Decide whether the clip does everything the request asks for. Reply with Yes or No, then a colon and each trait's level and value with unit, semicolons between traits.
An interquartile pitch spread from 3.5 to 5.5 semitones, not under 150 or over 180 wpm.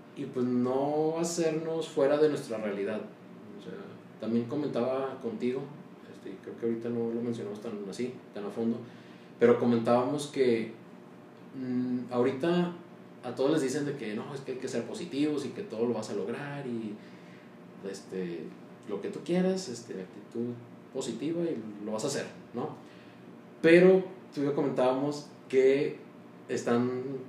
Yes: average, 5.1 semitones; average, 155 wpm